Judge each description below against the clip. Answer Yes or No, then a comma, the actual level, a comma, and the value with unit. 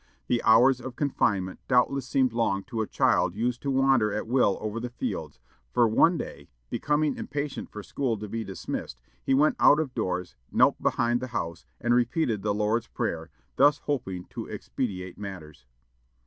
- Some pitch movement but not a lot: Yes, average, 4.6 semitones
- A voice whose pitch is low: Yes, low, 115 Hz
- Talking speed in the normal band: Yes, average, 175 wpm